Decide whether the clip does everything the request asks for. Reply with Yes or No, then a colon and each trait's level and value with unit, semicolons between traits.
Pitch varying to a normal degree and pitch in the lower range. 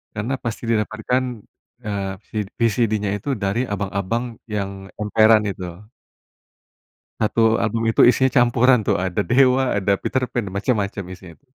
Yes: average, 3.2 semitones; low, 110 Hz